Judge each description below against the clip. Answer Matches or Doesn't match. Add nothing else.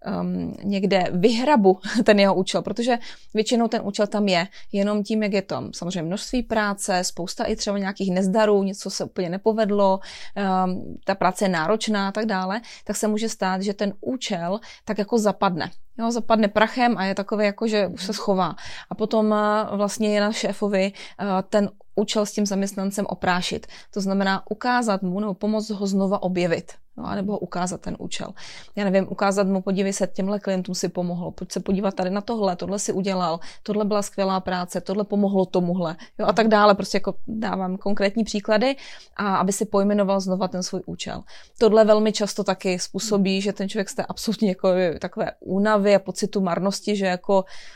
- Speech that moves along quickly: Matches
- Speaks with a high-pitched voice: Matches